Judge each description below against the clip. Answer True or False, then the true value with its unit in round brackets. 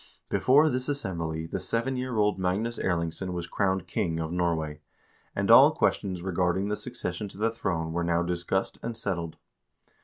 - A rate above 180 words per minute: False (165 wpm)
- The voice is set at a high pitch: False (95 Hz)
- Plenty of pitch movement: False (4.5 semitones)